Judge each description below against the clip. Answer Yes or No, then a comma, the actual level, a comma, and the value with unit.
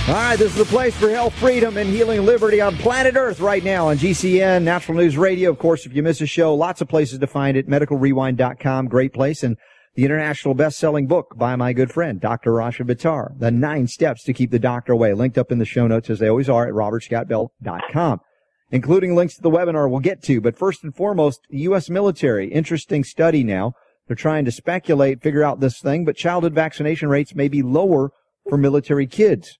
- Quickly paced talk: Yes, fast, 215 wpm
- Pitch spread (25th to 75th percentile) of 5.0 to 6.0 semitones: Yes, wide, 5.4 semitones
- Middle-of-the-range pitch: Yes, medium, 150 Hz